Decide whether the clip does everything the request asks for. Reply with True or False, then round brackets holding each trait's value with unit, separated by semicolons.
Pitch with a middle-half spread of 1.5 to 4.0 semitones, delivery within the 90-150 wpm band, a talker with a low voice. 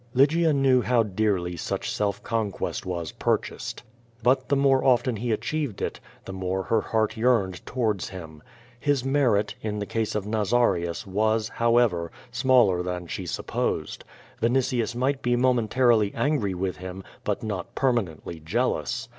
False (4.9 semitones; 145 wpm; 110 Hz)